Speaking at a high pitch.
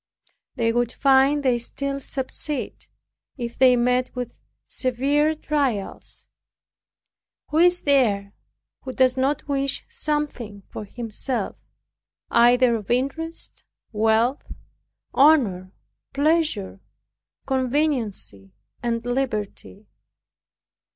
Yes: very high, 255 Hz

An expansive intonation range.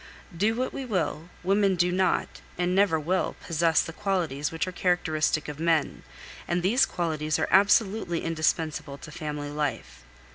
No: average, 3.5 semitones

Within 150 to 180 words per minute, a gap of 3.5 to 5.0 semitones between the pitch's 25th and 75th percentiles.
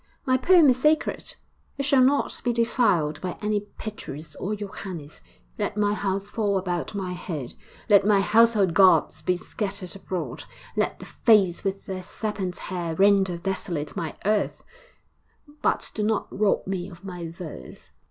No: average, 155 wpm; average, 3.1 semitones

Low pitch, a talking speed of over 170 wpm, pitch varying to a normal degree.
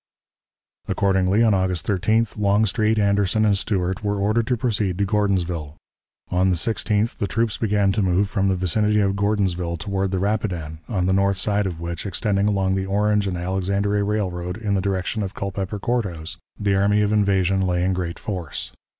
No: low, 100 Hz; average, 185 wpm; narrow, 2.1 semitones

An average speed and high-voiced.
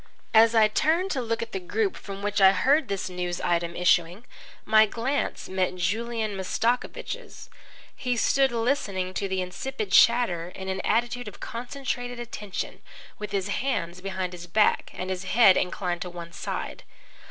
Yes: average, 165 wpm; high, 205 Hz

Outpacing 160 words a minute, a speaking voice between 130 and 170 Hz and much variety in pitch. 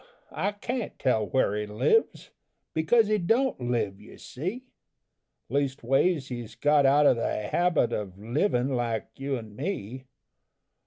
No: average, 140 wpm; low, 135 Hz; wide, 7.5 semitones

